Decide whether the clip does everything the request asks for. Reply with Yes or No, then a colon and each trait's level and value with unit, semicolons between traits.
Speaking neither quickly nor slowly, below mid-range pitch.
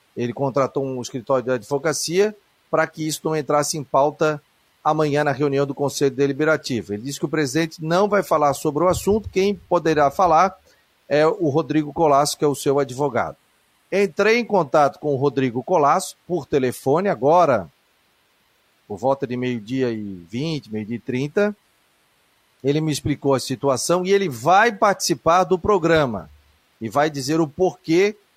No: average, 165 wpm; medium, 150 Hz